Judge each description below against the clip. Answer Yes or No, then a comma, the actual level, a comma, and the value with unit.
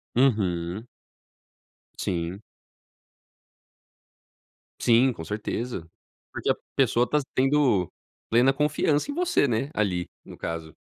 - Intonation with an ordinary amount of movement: No, wide, 7.0 semitones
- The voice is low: Yes, low, 115 Hz